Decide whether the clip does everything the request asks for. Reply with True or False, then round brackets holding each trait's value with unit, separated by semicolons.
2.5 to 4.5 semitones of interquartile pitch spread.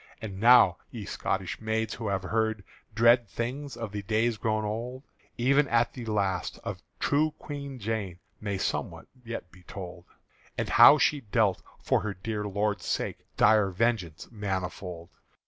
True (3.4 semitones)